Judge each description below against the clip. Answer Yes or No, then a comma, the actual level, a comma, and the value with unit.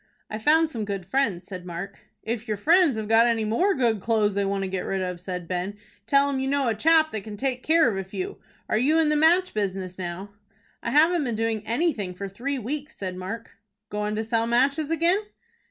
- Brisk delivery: Yes, fast, 225 wpm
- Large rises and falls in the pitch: Yes, wide, 6.4 semitones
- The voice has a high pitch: Yes, high, 225 Hz